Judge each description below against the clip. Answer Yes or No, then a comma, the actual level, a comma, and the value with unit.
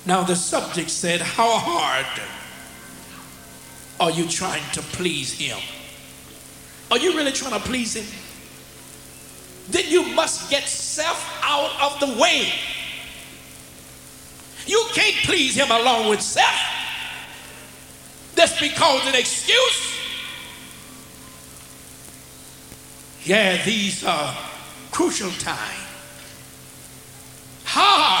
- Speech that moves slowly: Yes, slow, 95 wpm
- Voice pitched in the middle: Yes, medium, 165 Hz